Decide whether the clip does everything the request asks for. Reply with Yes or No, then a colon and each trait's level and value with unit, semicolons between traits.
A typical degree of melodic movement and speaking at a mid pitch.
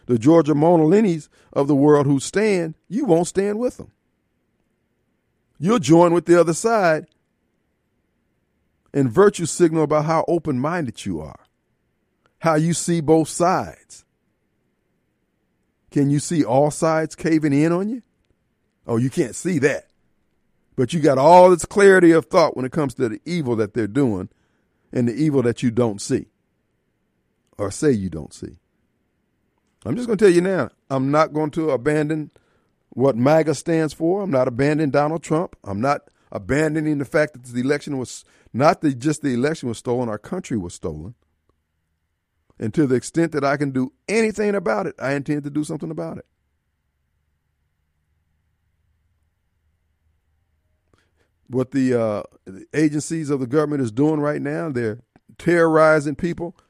No: wide, 5.9 semitones; medium, 145 Hz